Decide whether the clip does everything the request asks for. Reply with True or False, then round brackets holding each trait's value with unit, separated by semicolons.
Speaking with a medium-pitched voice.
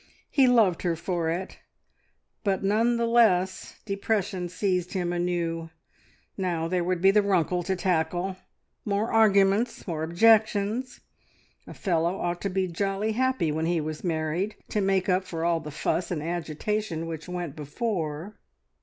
True (180 Hz)